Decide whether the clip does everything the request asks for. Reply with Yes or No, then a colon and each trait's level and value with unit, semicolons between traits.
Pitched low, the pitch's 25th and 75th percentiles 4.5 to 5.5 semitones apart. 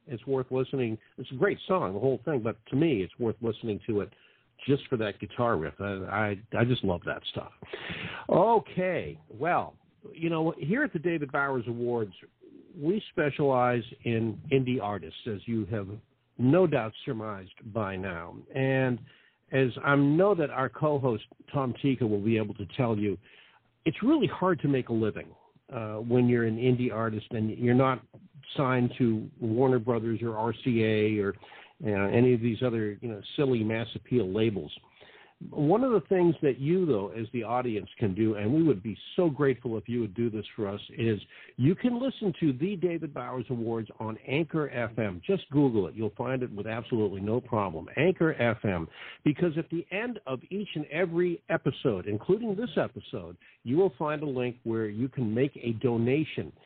Yes: low, 125 Hz; average, 4.8 semitones